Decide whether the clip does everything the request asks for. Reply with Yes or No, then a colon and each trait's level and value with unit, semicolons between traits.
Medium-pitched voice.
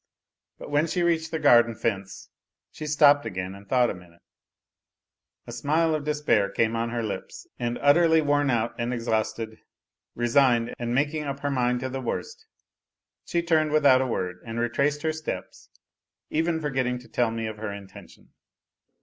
No: low, 125 Hz